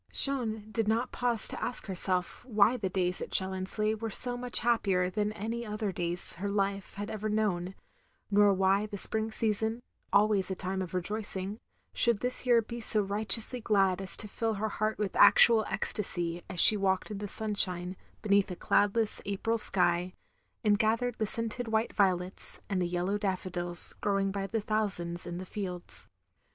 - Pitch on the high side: Yes, high, 205 Hz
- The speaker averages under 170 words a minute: No, average, 175 wpm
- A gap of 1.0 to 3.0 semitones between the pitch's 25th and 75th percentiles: Yes, average, 2.7 semitones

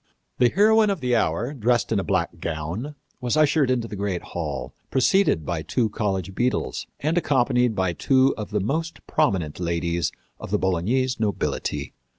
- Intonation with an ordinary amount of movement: No, wide, 7.1 semitones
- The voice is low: Yes, low, 110 Hz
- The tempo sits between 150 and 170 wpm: Yes, average, 165 wpm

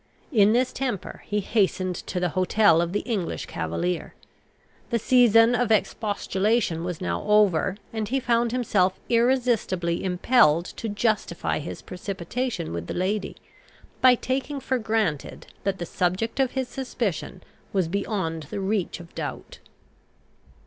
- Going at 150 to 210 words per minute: No, average, 140 wpm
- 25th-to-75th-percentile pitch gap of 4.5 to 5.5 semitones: Yes, average, 4.8 semitones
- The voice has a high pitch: Yes, high, 205 Hz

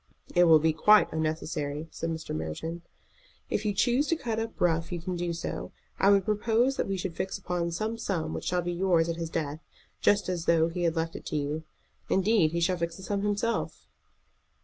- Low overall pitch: No, medium, 175 Hz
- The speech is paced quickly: Yes, fast, 215 wpm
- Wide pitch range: No, average, 3.7 semitones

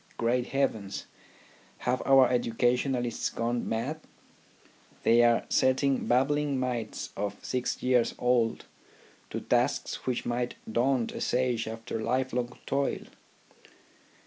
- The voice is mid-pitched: No, low, 125 Hz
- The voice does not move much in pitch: Yes, narrow, 1.8 semitones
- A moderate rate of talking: No, slow, 115 wpm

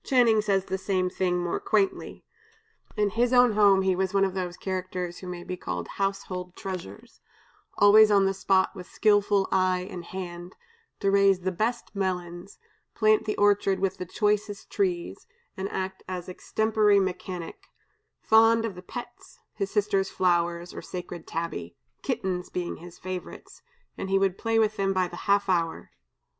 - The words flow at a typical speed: Yes, average, 165 wpm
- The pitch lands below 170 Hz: No, high, 190 Hz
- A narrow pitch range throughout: Yes, narrow, 2.3 semitones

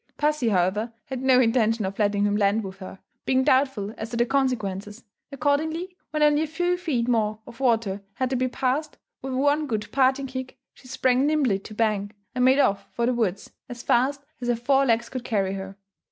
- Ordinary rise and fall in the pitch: Yes, average, 4.2 semitones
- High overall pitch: Yes, high, 245 Hz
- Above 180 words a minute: Yes, average, 200 wpm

